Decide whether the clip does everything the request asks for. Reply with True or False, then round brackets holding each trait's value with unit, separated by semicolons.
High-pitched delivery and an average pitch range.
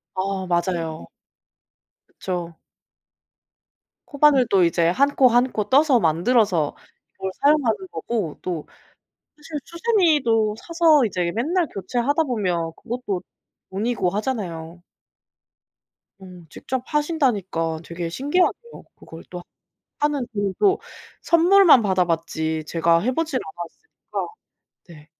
False (215 Hz; 8.8 semitones)